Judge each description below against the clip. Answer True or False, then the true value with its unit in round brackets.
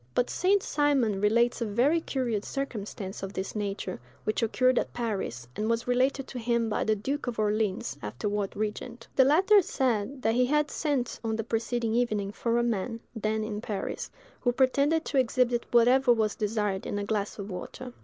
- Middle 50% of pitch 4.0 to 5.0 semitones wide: False (3.4 semitones)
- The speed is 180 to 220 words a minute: True (185 wpm)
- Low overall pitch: False (230 Hz)